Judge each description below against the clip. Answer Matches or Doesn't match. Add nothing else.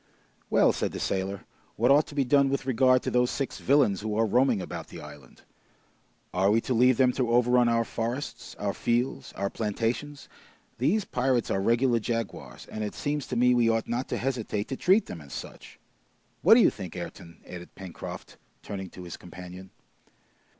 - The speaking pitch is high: Doesn't match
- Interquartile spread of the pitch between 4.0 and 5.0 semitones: Matches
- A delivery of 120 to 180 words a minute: Doesn't match